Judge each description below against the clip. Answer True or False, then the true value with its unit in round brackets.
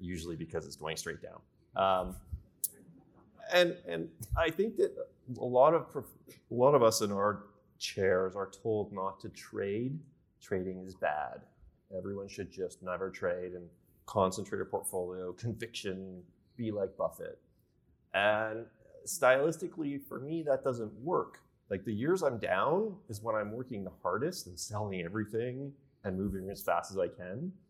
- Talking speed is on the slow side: False (155 wpm)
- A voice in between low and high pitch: False (110 Hz)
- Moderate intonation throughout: False (6.3 semitones)